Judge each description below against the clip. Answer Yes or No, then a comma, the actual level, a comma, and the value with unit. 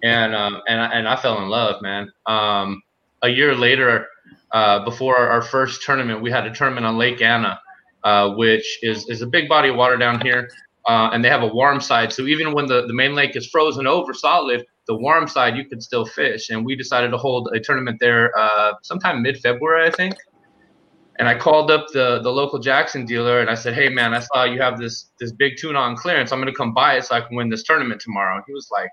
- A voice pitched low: Yes, low, 120 Hz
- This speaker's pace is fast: Yes, fast, 245 wpm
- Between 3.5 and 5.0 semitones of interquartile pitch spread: No, average, 2.8 semitones